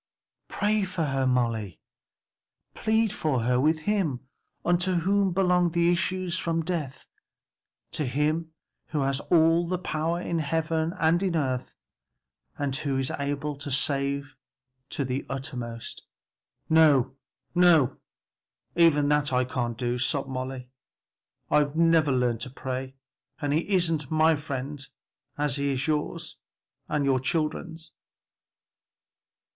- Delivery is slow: Yes, slow, 125 wpm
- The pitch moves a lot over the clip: No, average, 3.9 semitones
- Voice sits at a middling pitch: Yes, medium, 150 Hz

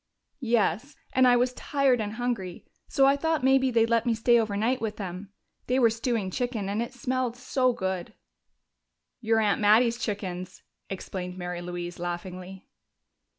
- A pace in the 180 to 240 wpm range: No, average, 155 wpm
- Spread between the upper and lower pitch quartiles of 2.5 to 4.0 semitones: No, average, 4.7 semitones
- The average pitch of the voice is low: No, high, 225 Hz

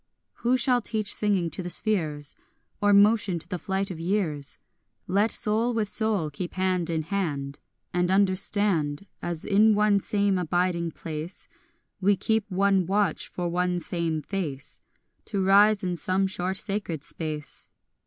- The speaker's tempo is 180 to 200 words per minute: No, average, 155 wpm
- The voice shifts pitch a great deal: No, average, 3.3 semitones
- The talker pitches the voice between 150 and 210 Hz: Yes, medium, 185 Hz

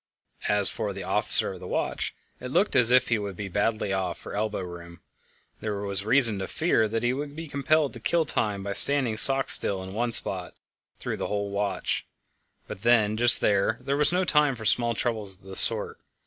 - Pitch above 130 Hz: No, low, 110 Hz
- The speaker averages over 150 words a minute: Yes, fast, 205 wpm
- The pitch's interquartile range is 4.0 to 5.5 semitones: Yes, average, 4.5 semitones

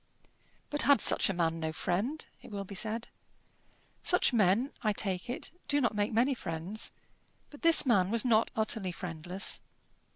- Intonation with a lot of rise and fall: No, average, 4.9 semitones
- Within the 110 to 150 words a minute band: No, average, 165 wpm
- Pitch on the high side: Yes, high, 215 Hz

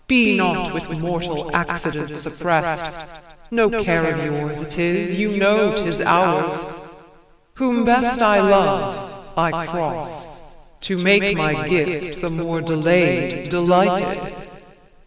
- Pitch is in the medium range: Yes, medium, 175 Hz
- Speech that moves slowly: Yes, slow, 120 wpm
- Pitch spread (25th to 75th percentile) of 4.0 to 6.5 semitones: No, average, 3.4 semitones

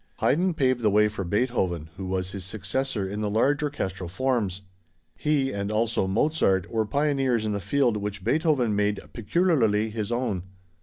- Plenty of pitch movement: No, average, 5.0 semitones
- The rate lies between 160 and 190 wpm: Yes, average, 165 wpm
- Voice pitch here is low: Yes, low, 110 Hz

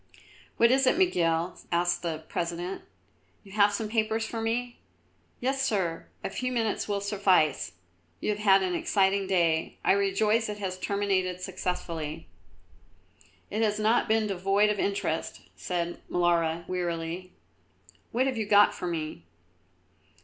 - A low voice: No, high, 195 Hz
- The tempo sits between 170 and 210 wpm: No, average, 140 wpm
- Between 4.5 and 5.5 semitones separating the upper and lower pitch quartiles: No, average, 3.7 semitones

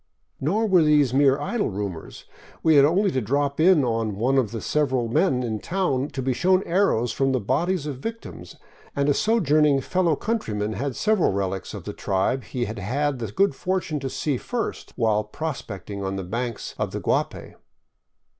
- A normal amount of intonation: No, wide, 6.1 semitones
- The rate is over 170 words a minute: Yes, average, 190 wpm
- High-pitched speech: No, low, 135 Hz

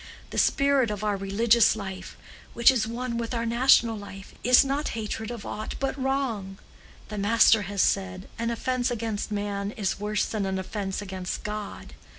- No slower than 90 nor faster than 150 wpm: No, average, 170 wpm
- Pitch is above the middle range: Yes, high, 215 Hz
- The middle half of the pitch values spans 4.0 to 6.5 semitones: No, average, 2.9 semitones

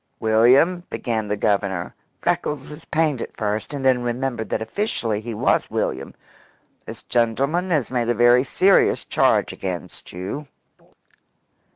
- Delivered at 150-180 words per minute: No, average, 140 wpm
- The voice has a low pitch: Yes, low, 120 Hz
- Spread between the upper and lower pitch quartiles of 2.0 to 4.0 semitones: No, average, 4.5 semitones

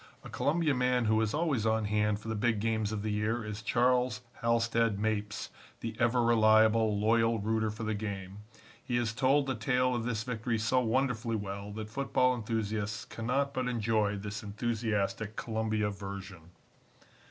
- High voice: No, low, 110 Hz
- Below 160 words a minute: No, average, 165 wpm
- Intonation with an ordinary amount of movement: No, narrow, 2.2 semitones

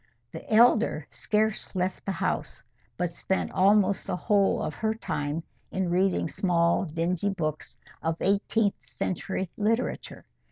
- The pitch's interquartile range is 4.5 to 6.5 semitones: No, average, 3.6 semitones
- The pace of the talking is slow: Yes, slow, 130 wpm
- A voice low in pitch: No, high, 190 Hz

